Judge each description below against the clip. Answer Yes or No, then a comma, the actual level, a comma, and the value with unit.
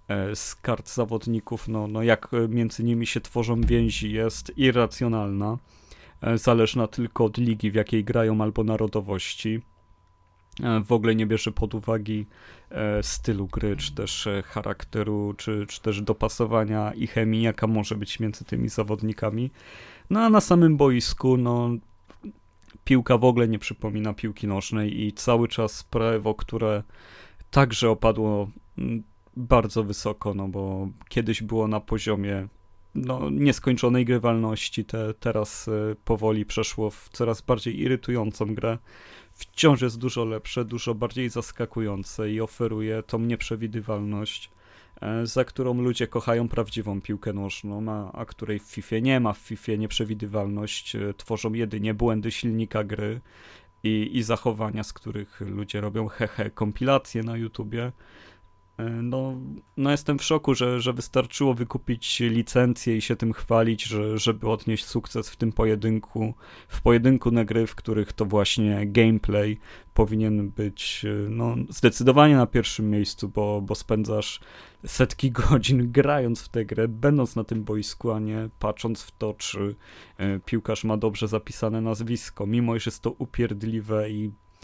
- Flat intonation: Yes, narrow, 1.9 semitones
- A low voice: Yes, low, 110 Hz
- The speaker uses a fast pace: No, average, 140 wpm